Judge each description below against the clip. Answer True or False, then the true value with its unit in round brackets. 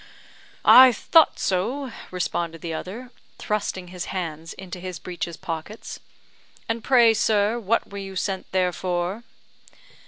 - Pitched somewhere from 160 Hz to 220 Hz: True (190 Hz)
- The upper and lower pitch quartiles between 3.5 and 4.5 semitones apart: True (4.2 semitones)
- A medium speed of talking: False (130 wpm)